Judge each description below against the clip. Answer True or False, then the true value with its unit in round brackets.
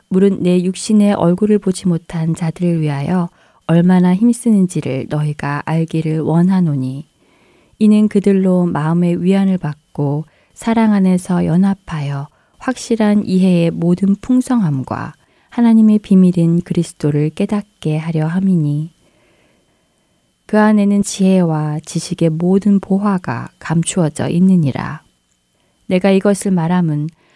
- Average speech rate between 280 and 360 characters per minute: False (270 characters per minute)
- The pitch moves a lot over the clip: False (3.8 semitones)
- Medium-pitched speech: True (180 Hz)